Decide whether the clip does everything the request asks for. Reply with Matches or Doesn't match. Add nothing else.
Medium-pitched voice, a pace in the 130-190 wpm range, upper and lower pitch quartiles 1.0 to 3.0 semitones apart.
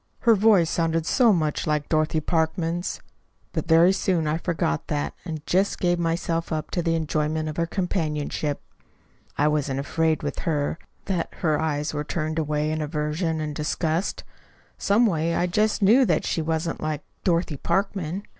Matches